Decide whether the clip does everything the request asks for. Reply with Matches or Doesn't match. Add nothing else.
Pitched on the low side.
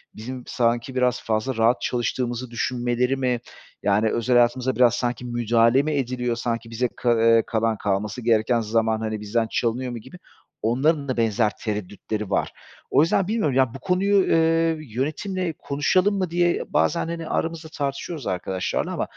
Matches